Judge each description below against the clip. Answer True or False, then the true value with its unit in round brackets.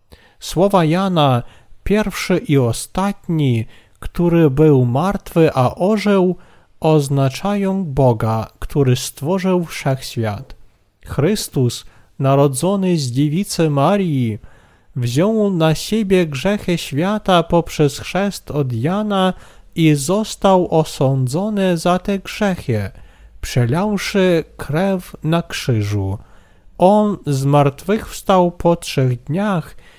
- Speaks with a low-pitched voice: False (160 Hz)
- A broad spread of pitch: True (6.5 semitones)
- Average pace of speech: False (90 wpm)